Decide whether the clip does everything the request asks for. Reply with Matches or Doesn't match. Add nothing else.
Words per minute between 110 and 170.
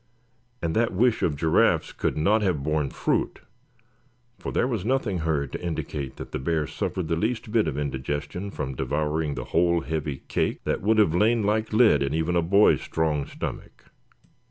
Doesn't match